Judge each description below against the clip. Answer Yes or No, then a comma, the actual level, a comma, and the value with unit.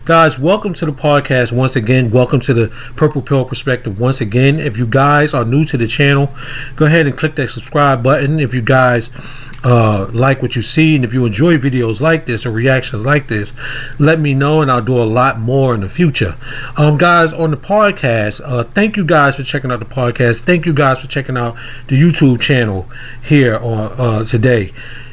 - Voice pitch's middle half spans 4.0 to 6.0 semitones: No, average, 3.4 semitones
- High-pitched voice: No, low, 130 Hz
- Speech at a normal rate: No, fast, 210 wpm